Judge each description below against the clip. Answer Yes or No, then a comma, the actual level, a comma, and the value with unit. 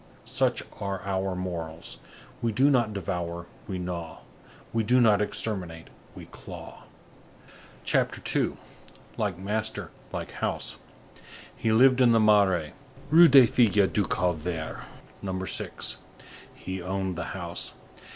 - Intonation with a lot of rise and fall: No, average, 3.8 semitones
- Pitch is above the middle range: No, very low, 95 Hz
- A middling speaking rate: No, slow, 120 wpm